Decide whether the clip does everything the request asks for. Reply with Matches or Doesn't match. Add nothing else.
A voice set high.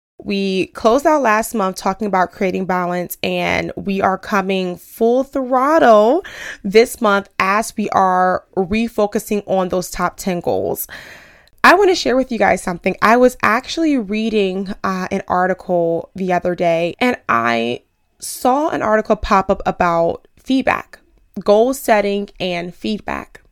Matches